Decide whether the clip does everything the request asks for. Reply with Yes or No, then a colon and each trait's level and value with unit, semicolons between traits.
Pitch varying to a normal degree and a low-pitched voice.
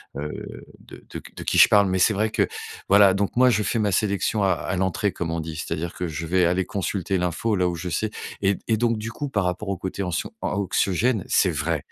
Yes: average, 3.0 semitones; very low, 95 Hz